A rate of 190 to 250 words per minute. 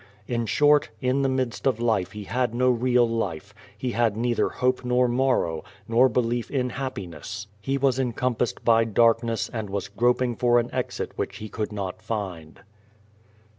No: average, 170 wpm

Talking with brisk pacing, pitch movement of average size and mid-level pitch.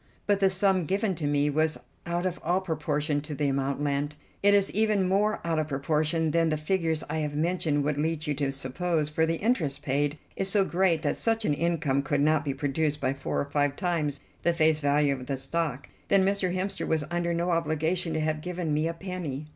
Yes: fast, 220 wpm; average, 3.4 semitones; medium, 155 Hz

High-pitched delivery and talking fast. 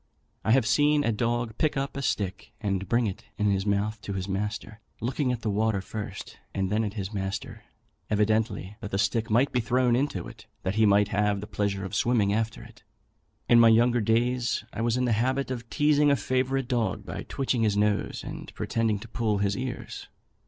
No: low, 110 Hz; fast, 210 wpm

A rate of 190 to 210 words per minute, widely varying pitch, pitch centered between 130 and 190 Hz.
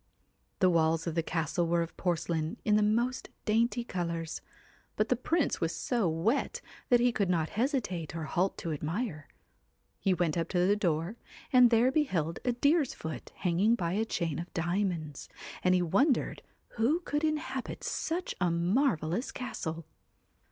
No: average, 165 wpm; wide, 6.4 semitones; medium, 185 Hz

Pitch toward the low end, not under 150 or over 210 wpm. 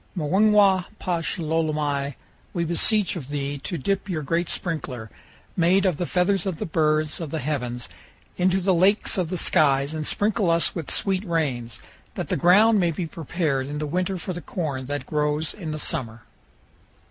No: medium, 165 Hz; average, 180 wpm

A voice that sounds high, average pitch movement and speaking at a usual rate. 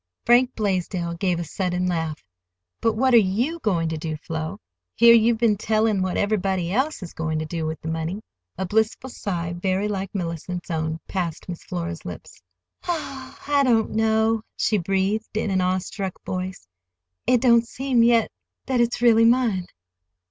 Yes: high, 195 Hz; average, 4.8 semitones; average, 170 wpm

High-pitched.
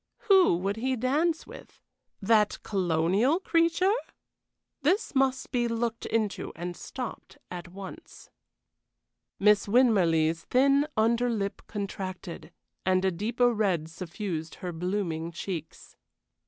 Yes: high, 210 Hz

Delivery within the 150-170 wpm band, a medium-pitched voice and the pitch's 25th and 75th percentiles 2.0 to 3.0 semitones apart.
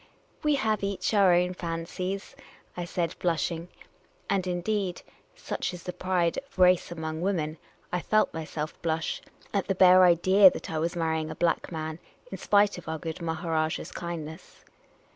Yes: average, 165 wpm; medium, 175 Hz; narrow, 2.5 semitones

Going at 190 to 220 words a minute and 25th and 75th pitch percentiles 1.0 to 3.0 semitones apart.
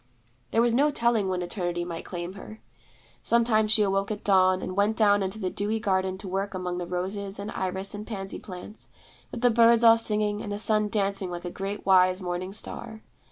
Yes: fast, 205 wpm; average, 2.7 semitones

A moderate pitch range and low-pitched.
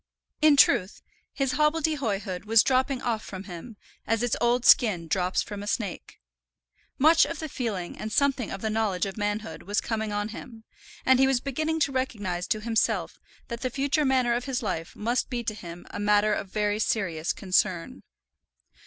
No: average, 4.2 semitones; high, 220 Hz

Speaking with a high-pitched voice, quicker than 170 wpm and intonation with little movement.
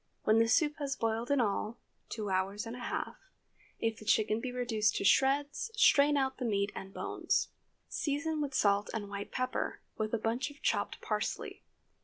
No: high, 230 Hz; average, 185 wpm; average, 4.6 semitones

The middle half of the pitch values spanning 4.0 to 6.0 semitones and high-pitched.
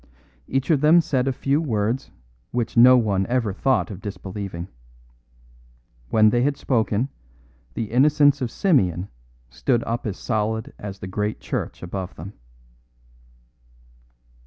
No: average, 4.7 semitones; low, 110 Hz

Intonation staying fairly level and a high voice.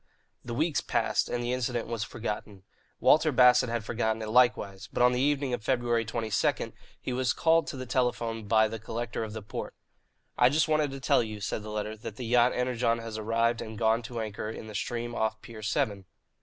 No: narrow, 2.3 semitones; low, 115 Hz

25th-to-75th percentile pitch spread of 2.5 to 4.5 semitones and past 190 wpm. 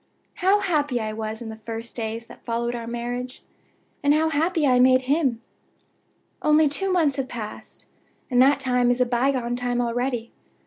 No: average, 3.5 semitones; average, 180 wpm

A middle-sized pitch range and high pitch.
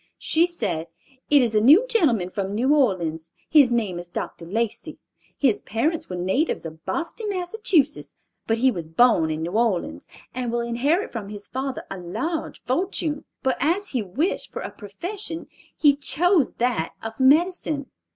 No: wide, 8.1 semitones; very high, 250 Hz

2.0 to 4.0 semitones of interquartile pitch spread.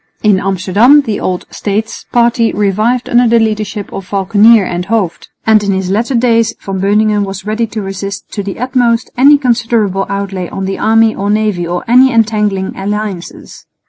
Yes: average, 2.8 semitones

